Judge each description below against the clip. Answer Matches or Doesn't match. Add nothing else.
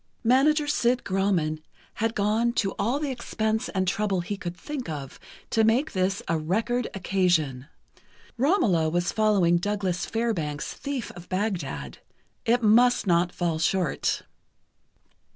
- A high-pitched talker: Matches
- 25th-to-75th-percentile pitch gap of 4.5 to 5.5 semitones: Matches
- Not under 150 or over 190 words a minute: Doesn't match